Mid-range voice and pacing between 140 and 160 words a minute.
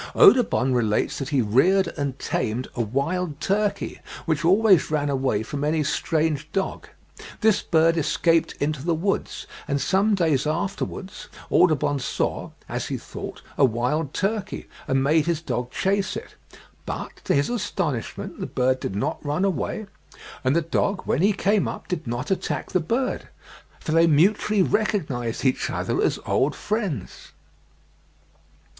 Yes: medium, 160 Hz; average, 150 wpm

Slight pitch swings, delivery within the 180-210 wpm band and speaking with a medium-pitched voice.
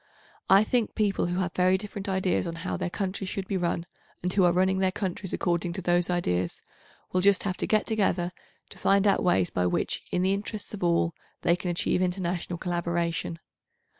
Yes: narrow, 2.0 semitones; average, 200 wpm; medium, 180 Hz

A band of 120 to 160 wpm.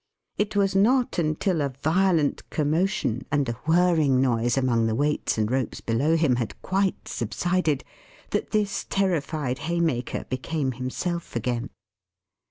Yes: slow, 135 wpm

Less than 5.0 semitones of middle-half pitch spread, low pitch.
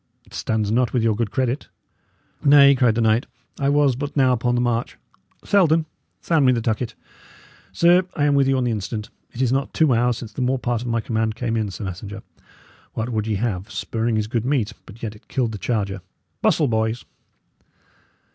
Yes: average, 3.2 semitones; low, 120 Hz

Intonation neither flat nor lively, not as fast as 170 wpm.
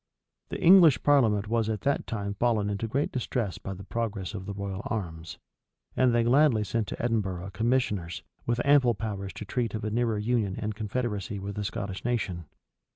No: average, 3.2 semitones; average, 185 wpm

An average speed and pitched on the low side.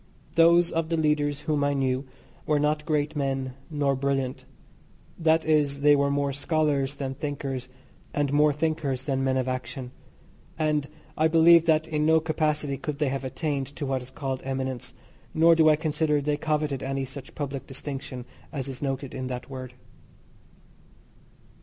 No: average, 165 wpm; medium, 145 Hz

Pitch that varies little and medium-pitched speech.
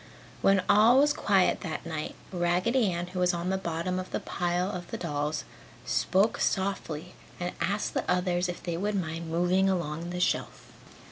Yes: narrow, 2.0 semitones; medium, 180 Hz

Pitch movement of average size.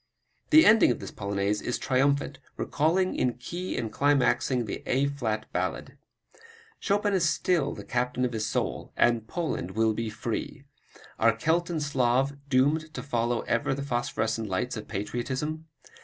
Yes: average, 4.7 semitones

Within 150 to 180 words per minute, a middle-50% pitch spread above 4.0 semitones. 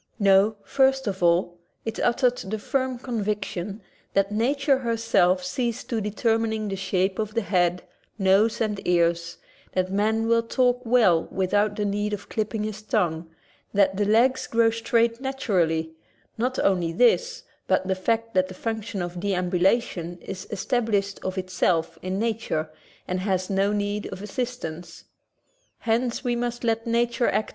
No: average, 155 wpm; average, 3.7 semitones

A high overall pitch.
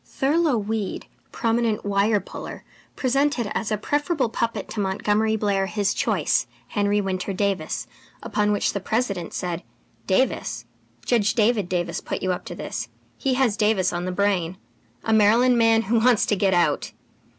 Yes: high, 210 Hz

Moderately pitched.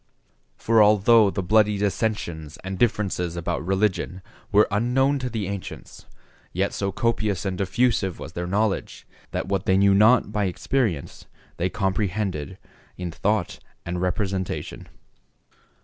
No: low, 100 Hz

